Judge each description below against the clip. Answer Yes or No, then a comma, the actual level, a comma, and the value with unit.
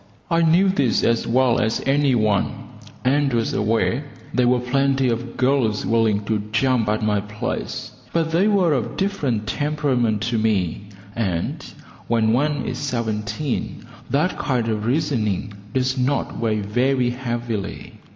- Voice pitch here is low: Yes, low, 120 Hz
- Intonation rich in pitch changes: No, average, 4.1 semitones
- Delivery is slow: No, average, 145 wpm